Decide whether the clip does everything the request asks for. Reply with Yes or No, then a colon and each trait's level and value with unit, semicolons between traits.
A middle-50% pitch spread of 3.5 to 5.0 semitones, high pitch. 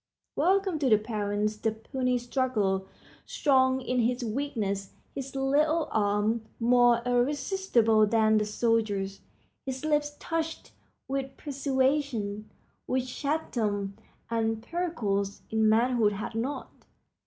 Yes: average, 4.2 semitones; high, 240 Hz